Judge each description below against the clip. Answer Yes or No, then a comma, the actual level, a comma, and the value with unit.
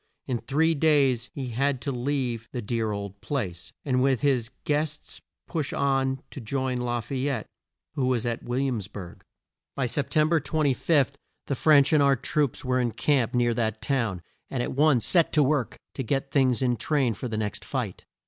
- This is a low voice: Yes, low, 130 Hz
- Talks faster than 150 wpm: Yes, average, 195 wpm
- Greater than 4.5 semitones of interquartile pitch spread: No, average, 3.1 semitones